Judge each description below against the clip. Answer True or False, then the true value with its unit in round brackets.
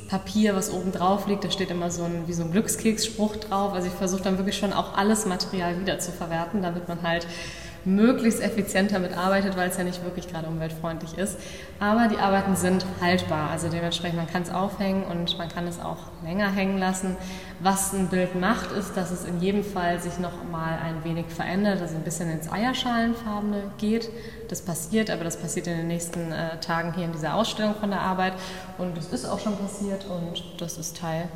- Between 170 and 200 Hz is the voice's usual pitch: True (185 Hz)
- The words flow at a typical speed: False (210 wpm)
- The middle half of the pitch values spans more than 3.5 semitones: False (2.7 semitones)